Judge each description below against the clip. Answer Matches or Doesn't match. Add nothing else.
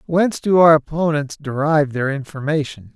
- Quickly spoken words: Doesn't match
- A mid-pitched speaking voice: Matches